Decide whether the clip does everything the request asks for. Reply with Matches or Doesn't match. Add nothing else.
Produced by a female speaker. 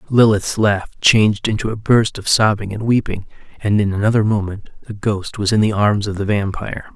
Doesn't match